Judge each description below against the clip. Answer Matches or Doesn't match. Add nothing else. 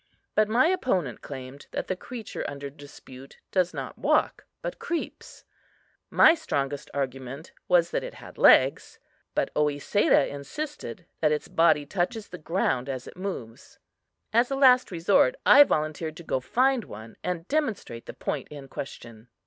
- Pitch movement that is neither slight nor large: Doesn't match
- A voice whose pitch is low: Doesn't match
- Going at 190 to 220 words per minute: Doesn't match